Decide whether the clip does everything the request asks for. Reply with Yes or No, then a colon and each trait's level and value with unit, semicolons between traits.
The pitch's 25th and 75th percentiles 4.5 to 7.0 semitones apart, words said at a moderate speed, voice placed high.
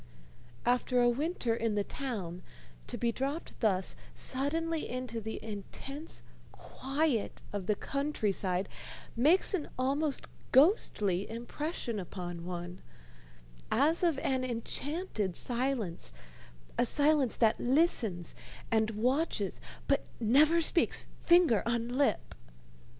No: wide, 5.5 semitones; slow, 110 wpm; high, 245 Hz